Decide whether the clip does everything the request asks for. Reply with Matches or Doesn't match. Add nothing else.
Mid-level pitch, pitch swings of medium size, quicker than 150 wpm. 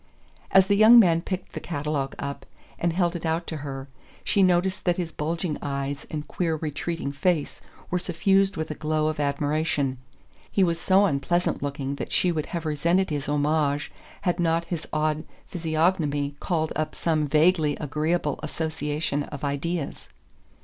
Matches